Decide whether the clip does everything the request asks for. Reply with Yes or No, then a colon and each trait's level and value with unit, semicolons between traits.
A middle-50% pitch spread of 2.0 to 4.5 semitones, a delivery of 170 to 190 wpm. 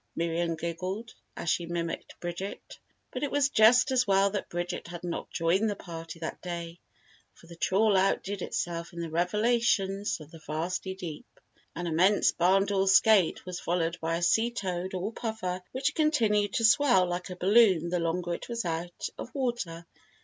Yes: average, 3.6 semitones; average, 180 wpm